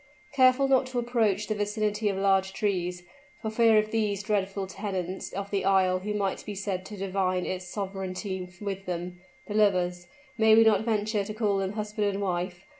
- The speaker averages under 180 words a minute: No, average, 190 wpm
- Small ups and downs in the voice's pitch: Yes, narrow, 2.1 semitones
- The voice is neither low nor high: No, high, 200 Hz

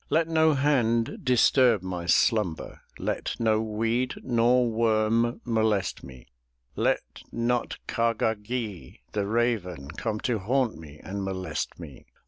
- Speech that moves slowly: Yes, slow, 130 wpm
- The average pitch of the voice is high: No, low, 110 Hz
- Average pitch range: Yes, average, 3.8 semitones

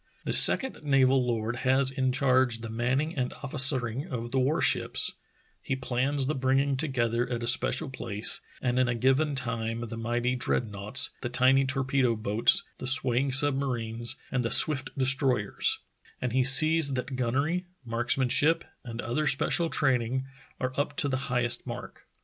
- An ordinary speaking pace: Yes, average, 160 wpm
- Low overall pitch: Yes, low, 130 Hz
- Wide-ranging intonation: No, narrow, 2.4 semitones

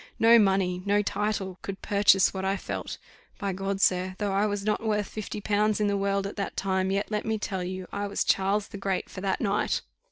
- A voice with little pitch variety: Yes, narrow, 1.4 semitones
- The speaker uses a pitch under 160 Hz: No, high, 200 Hz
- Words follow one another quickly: Yes, fast, 225 wpm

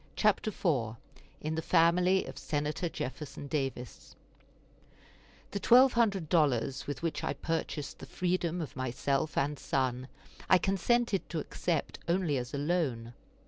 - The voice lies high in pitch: No, medium, 155 Hz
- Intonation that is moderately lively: Yes, average, 4.7 semitones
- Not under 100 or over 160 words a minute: Yes, average, 140 wpm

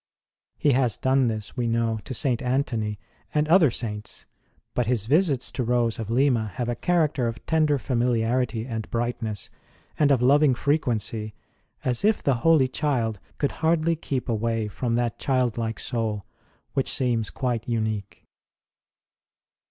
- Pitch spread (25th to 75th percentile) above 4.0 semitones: No, average, 3.4 semitones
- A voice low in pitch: Yes, low, 120 Hz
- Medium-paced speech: Yes, average, 145 wpm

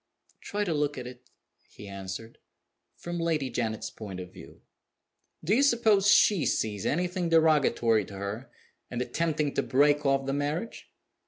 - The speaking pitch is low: No, medium, 145 Hz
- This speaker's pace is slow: No, average, 155 wpm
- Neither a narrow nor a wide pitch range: No, wide, 6.7 semitones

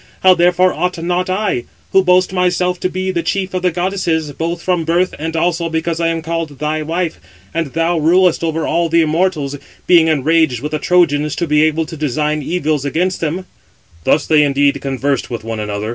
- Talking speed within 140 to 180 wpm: No, average, 195 wpm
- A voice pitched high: No, medium, 165 Hz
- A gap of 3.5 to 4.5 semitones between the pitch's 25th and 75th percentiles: No, average, 2.9 semitones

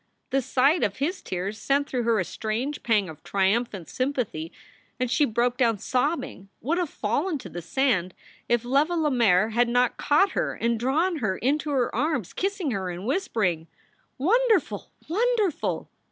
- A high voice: Yes, very high, 250 Hz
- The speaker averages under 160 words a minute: No, average, 165 wpm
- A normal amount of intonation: No, wide, 6.1 semitones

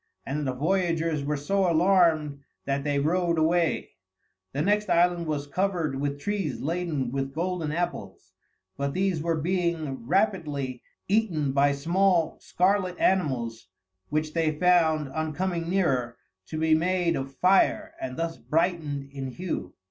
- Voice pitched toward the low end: No, medium, 160 Hz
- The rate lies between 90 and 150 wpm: Yes, average, 145 wpm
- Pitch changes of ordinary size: Yes, average, 4.1 semitones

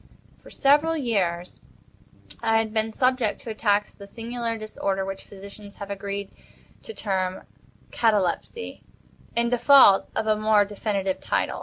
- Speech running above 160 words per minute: No, average, 140 wpm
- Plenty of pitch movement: No, average, 2.8 semitones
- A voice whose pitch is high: Yes, high, 215 Hz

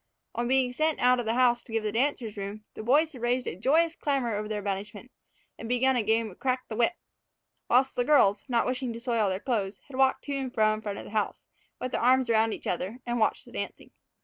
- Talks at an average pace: No, fast, 250 wpm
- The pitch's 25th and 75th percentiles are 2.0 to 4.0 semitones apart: Yes, average, 3.1 semitones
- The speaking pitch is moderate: No, high, 240 Hz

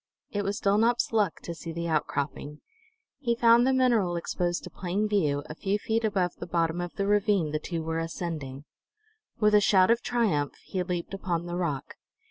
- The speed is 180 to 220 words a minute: Yes, average, 190 wpm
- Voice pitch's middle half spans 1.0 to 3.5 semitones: No, average, 4.3 semitones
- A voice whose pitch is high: No, medium, 180 Hz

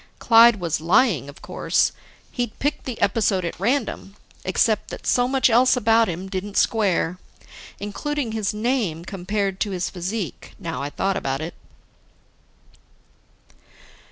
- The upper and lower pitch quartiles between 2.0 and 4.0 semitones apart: No, average, 4.4 semitones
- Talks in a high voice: Yes, high, 205 Hz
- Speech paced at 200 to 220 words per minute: No, slow, 135 wpm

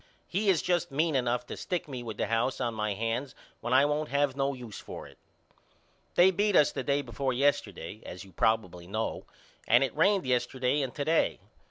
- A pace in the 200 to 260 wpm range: Yes, fast, 205 wpm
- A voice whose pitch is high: No, low, 130 Hz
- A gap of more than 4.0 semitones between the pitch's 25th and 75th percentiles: Yes, average, 4.5 semitones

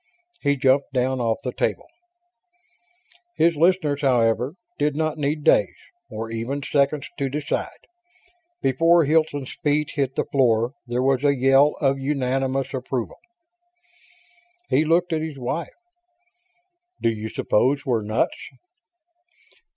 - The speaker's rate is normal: No, slow, 125 wpm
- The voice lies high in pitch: No, low, 135 Hz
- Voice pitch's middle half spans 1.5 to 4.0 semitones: Yes, average, 2.8 semitones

